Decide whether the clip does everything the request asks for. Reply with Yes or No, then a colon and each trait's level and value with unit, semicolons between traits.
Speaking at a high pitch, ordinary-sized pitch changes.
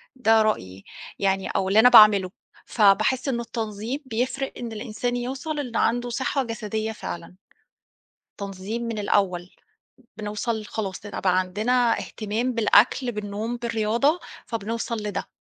Yes: high, 220 Hz; average, 3.0 semitones